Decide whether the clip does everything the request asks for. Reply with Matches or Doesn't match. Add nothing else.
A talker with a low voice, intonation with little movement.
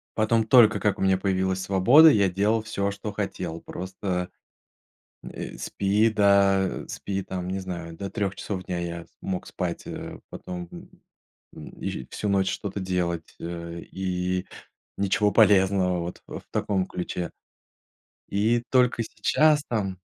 Matches